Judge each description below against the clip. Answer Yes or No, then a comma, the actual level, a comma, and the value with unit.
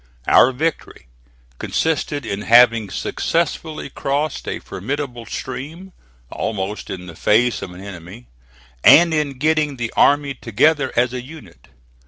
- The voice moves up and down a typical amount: No, wide, 6.0 semitones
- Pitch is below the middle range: Yes, low, 125 Hz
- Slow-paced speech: Yes, slow, 130 wpm